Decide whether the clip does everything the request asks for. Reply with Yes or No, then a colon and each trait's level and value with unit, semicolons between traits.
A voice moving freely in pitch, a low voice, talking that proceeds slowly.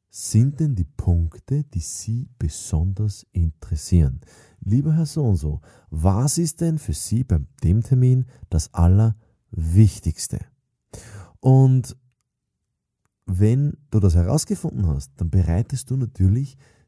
Yes: wide, 6.7 semitones; low, 105 Hz; slow, 115 wpm